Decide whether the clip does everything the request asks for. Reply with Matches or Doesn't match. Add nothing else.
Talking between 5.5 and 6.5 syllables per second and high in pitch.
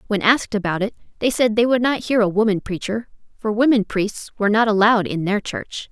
Matches